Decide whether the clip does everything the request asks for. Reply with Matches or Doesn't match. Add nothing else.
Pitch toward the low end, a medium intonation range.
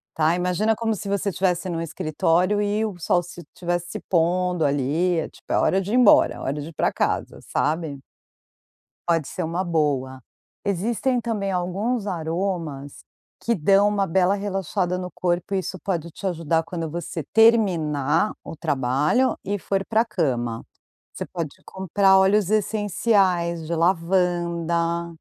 Doesn't match